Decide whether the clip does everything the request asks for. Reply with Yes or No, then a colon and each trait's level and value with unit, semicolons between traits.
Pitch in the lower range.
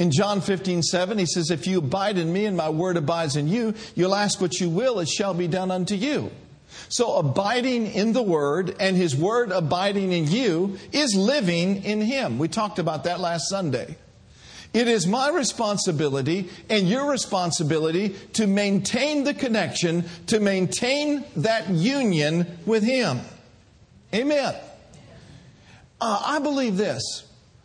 No: high, 195 Hz